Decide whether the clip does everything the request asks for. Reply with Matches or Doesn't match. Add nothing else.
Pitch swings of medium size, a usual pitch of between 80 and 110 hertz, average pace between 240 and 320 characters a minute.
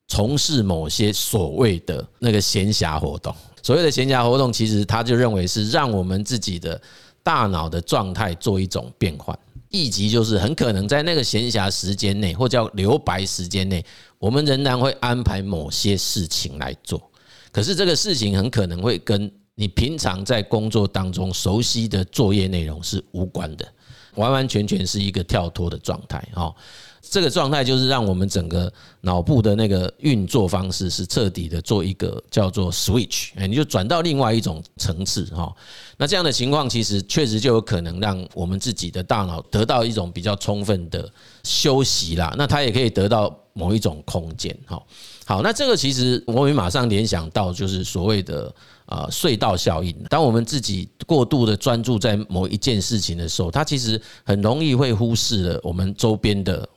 Matches